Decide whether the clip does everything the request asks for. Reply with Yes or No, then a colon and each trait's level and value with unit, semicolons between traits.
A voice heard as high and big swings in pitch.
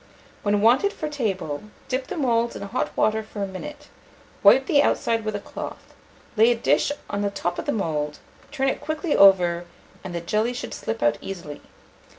Yes: high, 215 Hz; wide, 5.8 semitones